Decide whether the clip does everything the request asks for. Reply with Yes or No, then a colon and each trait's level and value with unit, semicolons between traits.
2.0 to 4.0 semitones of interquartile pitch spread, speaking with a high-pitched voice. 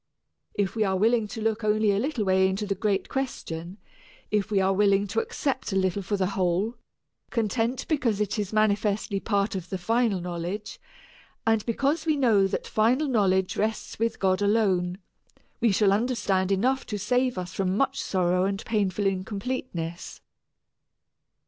Yes: average, 3.0 semitones; high, 205 Hz